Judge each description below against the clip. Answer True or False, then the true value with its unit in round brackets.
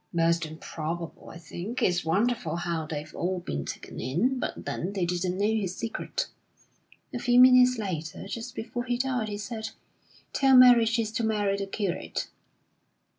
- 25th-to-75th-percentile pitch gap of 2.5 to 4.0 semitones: False (5.6 semitones)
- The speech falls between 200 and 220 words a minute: False (165 wpm)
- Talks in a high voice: True (200 Hz)